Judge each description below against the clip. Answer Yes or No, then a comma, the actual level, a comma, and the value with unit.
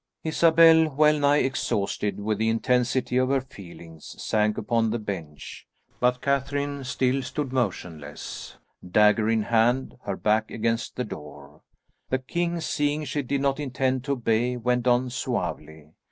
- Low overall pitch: Yes, low, 125 Hz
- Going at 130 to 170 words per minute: Yes, average, 140 wpm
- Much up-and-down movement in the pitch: No, average, 4.6 semitones